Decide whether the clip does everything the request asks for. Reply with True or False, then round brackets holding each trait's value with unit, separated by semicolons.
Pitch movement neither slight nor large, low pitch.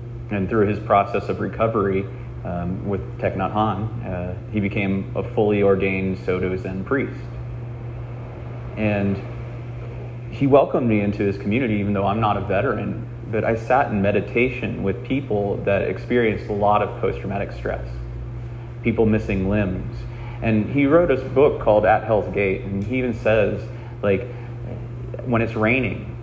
True (3.0 semitones; 110 Hz)